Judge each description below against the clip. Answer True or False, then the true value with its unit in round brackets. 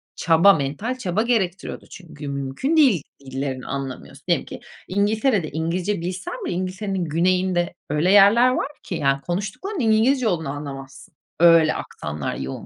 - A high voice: False (175 Hz)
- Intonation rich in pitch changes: True (6.1 semitones)